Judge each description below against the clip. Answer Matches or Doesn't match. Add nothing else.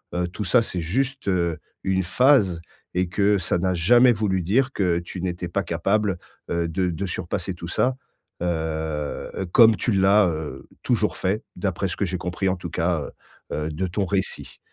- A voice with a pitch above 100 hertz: Doesn't match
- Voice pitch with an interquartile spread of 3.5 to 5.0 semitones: Doesn't match